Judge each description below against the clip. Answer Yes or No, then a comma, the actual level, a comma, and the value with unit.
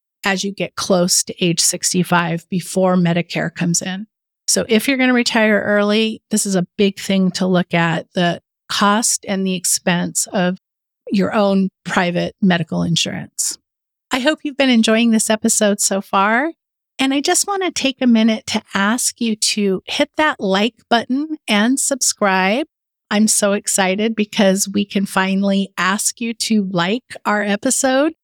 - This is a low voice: No, high, 205 Hz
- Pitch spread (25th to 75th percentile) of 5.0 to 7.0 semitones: No, average, 3.7 semitones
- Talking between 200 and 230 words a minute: No, average, 165 wpm